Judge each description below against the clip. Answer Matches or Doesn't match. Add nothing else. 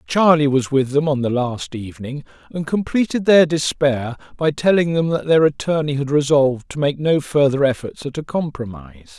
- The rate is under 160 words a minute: Doesn't match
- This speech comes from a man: Matches